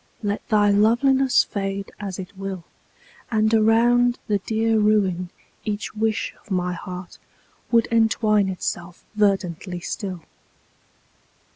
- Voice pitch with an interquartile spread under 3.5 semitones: Yes, average, 2.7 semitones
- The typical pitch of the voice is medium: No, high, 205 Hz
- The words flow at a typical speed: No, slow, 115 wpm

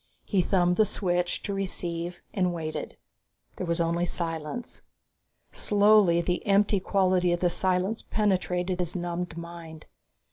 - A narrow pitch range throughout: Yes, narrow, 2.2 semitones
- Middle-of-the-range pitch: Yes, medium, 180 Hz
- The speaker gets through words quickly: No, slow, 135 wpm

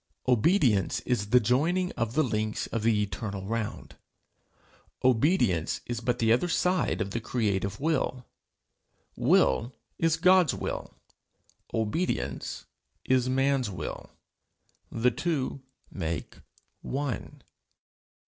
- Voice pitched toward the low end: Yes, low, 120 Hz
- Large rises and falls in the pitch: No, average, 5.0 semitones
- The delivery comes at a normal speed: No, slow, 110 wpm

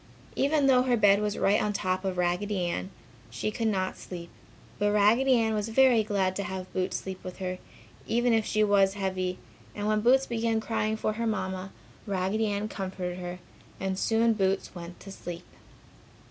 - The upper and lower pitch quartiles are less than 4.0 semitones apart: Yes, average, 3.0 semitones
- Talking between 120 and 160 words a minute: No, average, 185 wpm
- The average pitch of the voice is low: No, high, 205 Hz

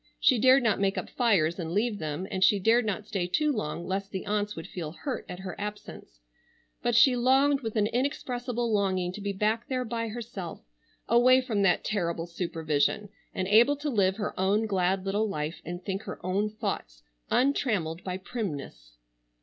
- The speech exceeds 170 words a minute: Yes, average, 185 wpm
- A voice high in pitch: Yes, high, 205 Hz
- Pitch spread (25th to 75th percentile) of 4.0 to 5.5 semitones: Yes, average, 4.6 semitones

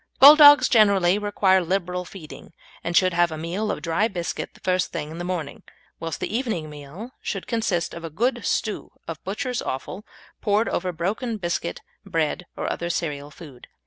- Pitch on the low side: No, medium, 180 Hz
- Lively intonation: No, average, 4.2 semitones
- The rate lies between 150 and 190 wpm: Yes, average, 175 wpm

